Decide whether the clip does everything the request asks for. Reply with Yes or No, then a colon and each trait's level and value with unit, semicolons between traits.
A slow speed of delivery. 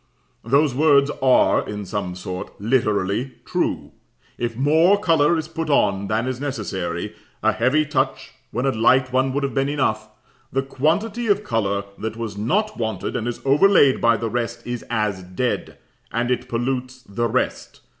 No: average, 165 wpm